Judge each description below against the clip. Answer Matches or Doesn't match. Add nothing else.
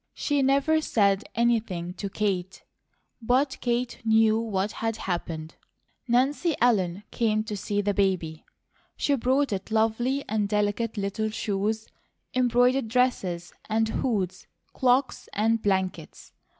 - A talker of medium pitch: Doesn't match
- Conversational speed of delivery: Doesn't match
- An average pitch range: Matches